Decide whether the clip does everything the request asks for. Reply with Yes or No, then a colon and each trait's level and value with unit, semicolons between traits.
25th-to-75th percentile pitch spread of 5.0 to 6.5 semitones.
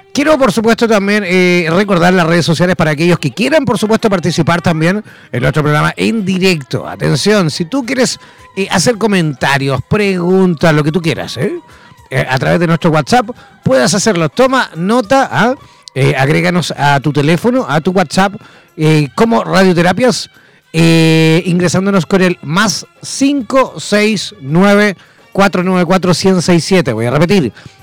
No: average, 4.3 semitones